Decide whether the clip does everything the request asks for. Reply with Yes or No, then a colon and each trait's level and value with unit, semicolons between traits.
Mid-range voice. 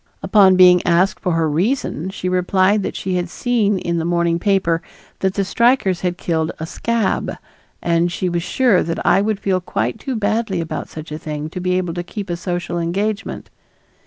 Yes: medium, 180 Hz